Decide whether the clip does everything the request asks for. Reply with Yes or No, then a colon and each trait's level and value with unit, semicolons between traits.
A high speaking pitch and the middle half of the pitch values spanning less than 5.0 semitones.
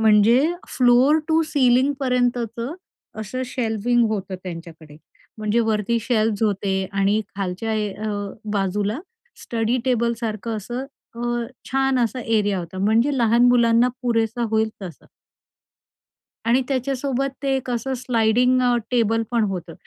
Yes: high, 230 Hz; average, 2.9 semitones